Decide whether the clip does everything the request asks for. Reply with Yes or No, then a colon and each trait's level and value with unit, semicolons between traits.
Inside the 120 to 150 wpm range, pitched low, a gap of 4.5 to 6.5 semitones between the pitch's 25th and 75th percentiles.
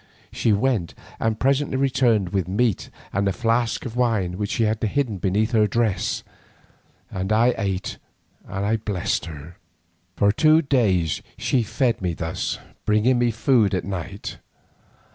No: average, 145 wpm; low, 110 Hz; average, 4.0 semitones